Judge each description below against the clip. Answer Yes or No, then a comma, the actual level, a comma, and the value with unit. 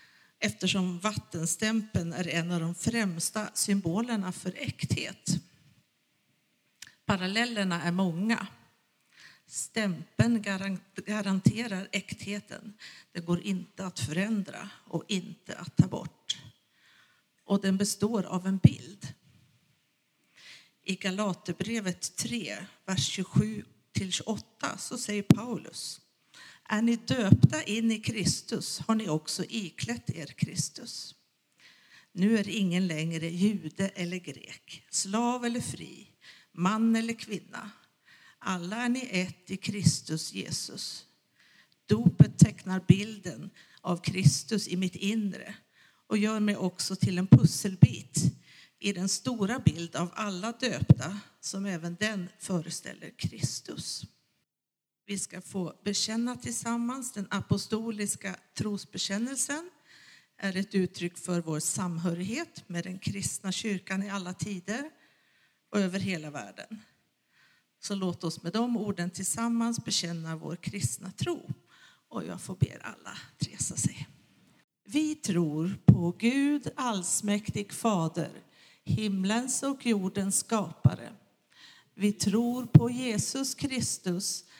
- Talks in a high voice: Yes, high, 195 Hz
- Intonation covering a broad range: No, average, 3.7 semitones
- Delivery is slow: Yes, slow, 110 wpm